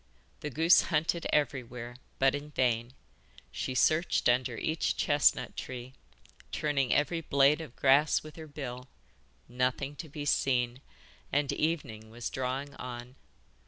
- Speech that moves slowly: Yes, slow, 130 wpm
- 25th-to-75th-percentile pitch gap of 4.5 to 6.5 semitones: No, average, 3.3 semitones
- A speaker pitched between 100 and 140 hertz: Yes, low, 135 Hz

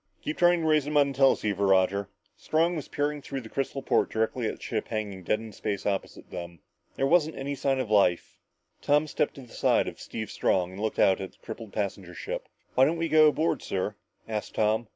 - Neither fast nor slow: No, fast, 225 wpm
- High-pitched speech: No, low, 115 Hz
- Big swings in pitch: Yes, wide, 6.6 semitones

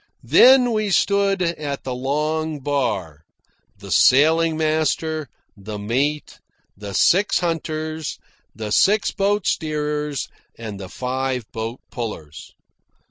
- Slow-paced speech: Yes, slow, 110 wpm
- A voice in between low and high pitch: Yes, medium, 150 Hz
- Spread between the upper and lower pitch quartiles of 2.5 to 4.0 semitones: No, wide, 5.4 semitones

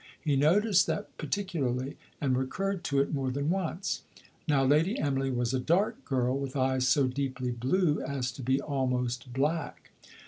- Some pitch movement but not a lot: Yes, average, 3.8 semitones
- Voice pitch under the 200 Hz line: Yes, medium, 140 Hz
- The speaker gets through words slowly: No, average, 165 wpm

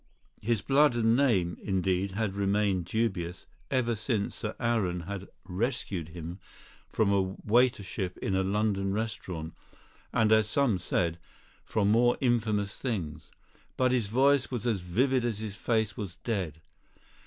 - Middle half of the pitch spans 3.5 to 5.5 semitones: Yes, average, 3.9 semitones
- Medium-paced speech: Yes, average, 145 wpm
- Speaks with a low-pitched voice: Yes, low, 105 Hz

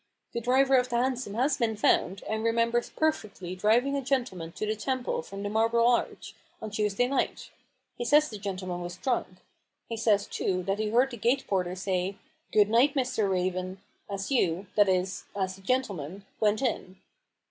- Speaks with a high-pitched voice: Yes, high, 215 Hz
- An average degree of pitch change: Yes, average, 4.4 semitones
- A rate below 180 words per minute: No, average, 190 wpm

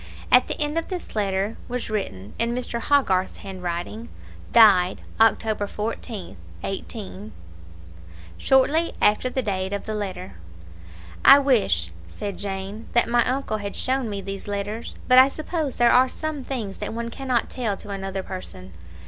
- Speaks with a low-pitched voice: No, high, 215 Hz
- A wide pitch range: No, average, 4.6 semitones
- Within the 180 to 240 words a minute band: No, average, 160 wpm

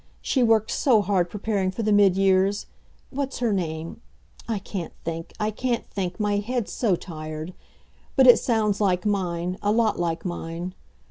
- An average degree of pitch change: Yes, average, 3.6 semitones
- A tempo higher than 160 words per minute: Yes, average, 170 wpm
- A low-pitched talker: No, high, 200 Hz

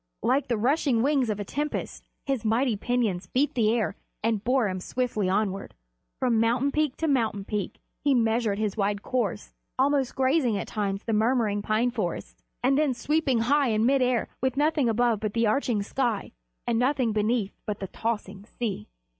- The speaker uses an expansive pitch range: No, average, 3.7 semitones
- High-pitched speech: Yes, high, 235 Hz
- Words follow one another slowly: No, average, 180 wpm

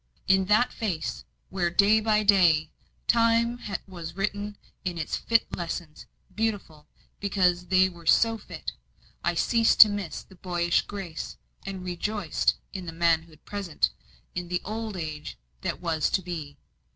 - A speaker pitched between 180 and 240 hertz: Yes, medium, 185 Hz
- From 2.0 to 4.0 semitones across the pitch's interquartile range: Yes, average, 3.6 semitones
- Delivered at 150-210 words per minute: No, average, 140 wpm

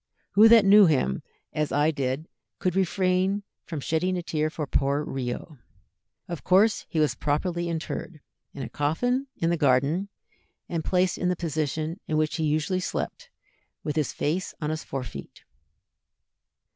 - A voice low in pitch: No, medium, 160 Hz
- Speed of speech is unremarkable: Yes, average, 160 wpm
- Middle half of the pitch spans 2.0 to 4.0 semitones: Yes, average, 3.7 semitones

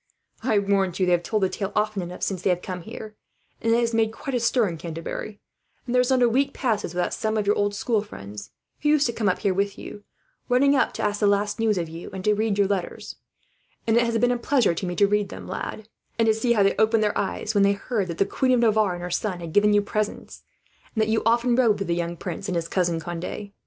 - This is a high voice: Yes, high, 205 Hz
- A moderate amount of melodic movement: Yes, average, 3.5 semitones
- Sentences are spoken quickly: Yes, fast, 275 wpm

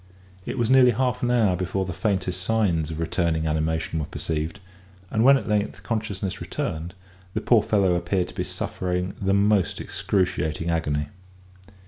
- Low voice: Yes, very low, 95 Hz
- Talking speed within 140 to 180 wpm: Yes, average, 160 wpm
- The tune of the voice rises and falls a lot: No, average, 4.7 semitones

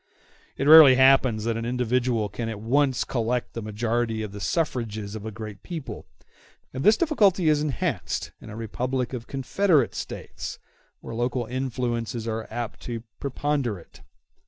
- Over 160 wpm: No, average, 155 wpm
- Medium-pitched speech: No, low, 120 Hz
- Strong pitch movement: No, average, 3.3 semitones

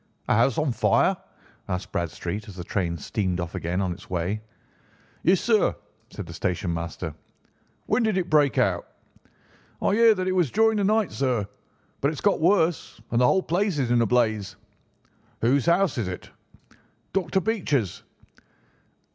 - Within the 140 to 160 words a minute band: No, average, 170 wpm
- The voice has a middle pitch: No, low, 125 Hz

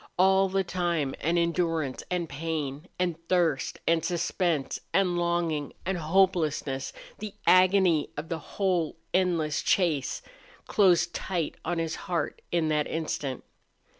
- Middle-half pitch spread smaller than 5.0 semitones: Yes, average, 2.7 semitones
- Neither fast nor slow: No, slow, 130 wpm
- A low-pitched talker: No, medium, 170 Hz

